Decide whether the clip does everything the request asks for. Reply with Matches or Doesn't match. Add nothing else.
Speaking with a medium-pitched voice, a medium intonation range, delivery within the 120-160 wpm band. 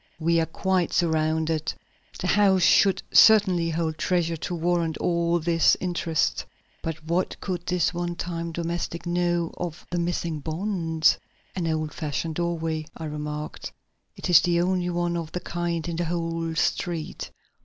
Doesn't match